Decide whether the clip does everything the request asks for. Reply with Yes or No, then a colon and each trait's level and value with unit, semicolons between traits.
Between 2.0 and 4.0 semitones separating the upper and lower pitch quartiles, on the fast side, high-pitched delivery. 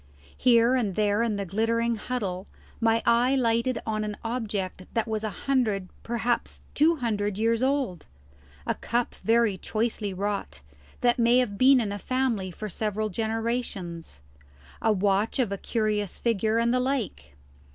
No: average, 2.8 semitones; average, 155 wpm; high, 225 Hz